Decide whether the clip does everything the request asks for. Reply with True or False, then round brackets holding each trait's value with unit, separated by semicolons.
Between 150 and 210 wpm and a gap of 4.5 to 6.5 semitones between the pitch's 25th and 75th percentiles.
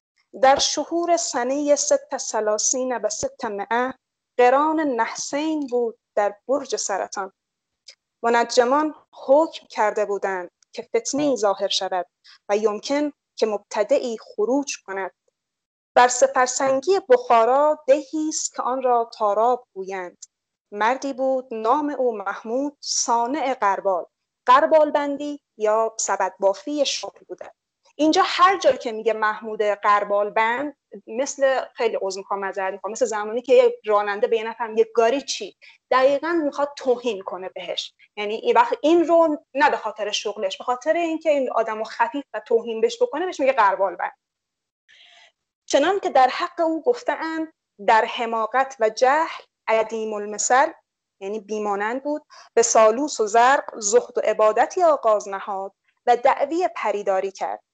False (140 wpm; 5.5 semitones)